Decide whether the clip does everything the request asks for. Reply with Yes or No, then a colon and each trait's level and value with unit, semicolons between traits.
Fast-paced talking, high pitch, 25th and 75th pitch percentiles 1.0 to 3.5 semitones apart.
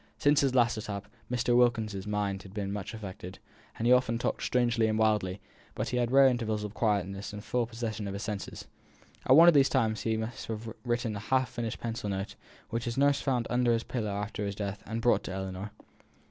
No: fast, 215 wpm; low, 110 Hz; average, 2.9 semitones